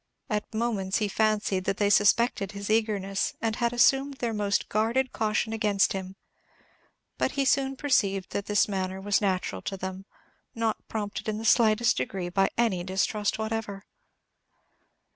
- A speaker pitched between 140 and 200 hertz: No, high, 210 Hz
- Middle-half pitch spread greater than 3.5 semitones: No, narrow, 2.5 semitones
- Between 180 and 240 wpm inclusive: No, average, 155 wpm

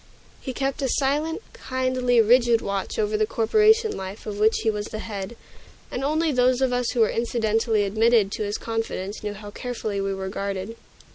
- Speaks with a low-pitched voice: No, high, 225 Hz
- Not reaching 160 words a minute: No, average, 190 wpm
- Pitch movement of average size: Yes, average, 3.6 semitones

